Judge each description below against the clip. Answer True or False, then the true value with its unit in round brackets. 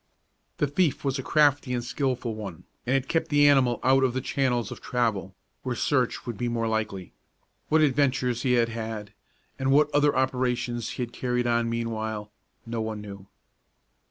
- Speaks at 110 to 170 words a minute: False (180 wpm)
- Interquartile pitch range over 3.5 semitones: False (2.9 semitones)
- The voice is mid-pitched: False (125 Hz)